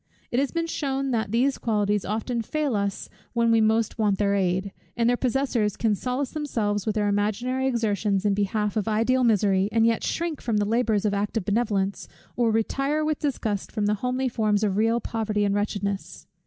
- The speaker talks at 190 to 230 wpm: Yes, average, 195 wpm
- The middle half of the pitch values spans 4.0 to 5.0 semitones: No, average, 3.3 semitones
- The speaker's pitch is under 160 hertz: No, high, 220 Hz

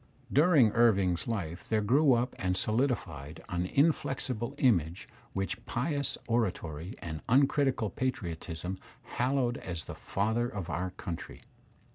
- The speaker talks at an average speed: No, slow, 120 wpm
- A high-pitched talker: No, low, 110 Hz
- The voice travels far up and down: Yes, wide, 6.2 semitones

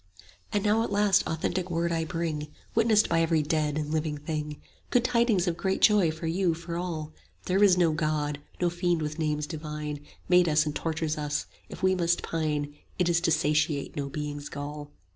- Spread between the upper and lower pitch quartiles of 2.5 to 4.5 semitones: Yes, average, 2.8 semitones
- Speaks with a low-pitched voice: No, medium, 160 Hz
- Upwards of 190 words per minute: Yes, average, 200 wpm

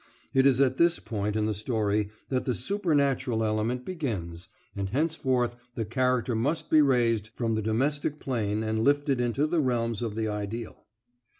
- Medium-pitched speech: No, low, 120 Hz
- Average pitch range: Yes, average, 4.0 semitones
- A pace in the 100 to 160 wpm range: No, average, 170 wpm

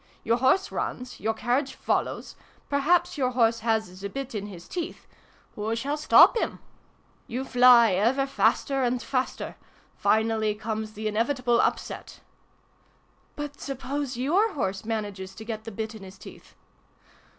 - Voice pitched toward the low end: No, high, 235 Hz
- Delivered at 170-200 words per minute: No, average, 150 wpm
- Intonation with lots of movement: No, average, 3.9 semitones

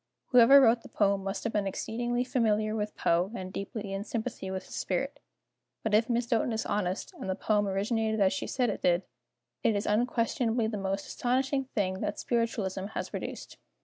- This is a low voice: No, high, 215 Hz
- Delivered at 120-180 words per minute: No, average, 190 wpm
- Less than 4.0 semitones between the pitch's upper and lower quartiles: Yes, average, 3.4 semitones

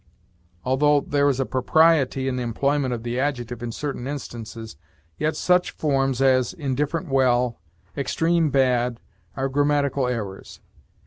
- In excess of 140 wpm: No, slow, 135 wpm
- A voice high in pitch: No, low, 135 Hz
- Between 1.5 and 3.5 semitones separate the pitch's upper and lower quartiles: Yes, average, 2.8 semitones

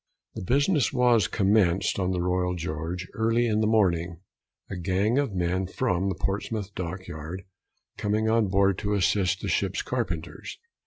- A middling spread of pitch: Yes, average, 3.4 semitones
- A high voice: No, very low, 95 Hz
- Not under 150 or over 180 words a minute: Yes, average, 160 wpm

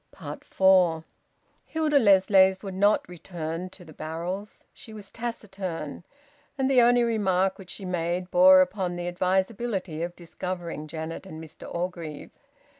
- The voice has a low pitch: No, medium, 185 Hz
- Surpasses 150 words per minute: No, slow, 135 wpm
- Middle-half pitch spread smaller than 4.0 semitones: Yes, narrow, 2.5 semitones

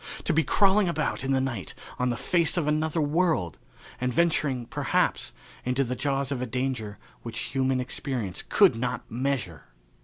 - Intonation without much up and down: No, average, 3.6 semitones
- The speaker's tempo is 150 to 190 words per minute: Yes, average, 165 wpm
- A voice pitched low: Yes, low, 130 Hz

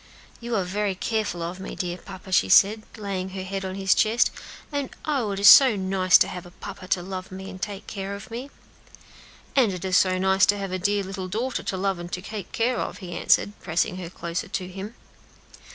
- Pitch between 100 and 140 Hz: No, high, 190 Hz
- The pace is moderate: No, fast, 225 wpm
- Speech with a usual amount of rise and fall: No, narrow, 2.0 semitones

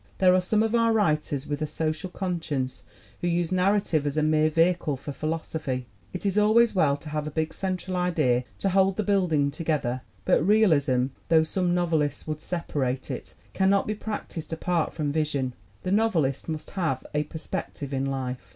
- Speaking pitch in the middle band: Yes, medium, 160 Hz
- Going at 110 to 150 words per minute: No, average, 190 wpm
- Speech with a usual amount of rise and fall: Yes, average, 4.2 semitones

